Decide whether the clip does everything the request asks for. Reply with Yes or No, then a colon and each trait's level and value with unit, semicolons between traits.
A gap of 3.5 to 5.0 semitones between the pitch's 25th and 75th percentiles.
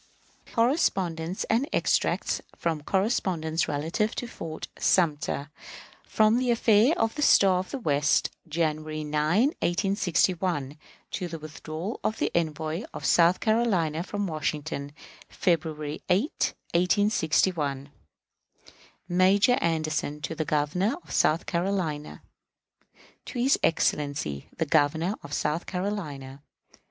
Yes: average, 4.6 semitones